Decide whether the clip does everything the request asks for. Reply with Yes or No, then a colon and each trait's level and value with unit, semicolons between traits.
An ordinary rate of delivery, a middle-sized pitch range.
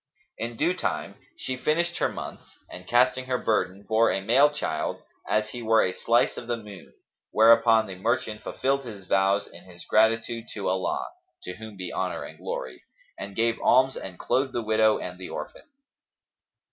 Yes: average, 180 wpm; average, 4.1 semitones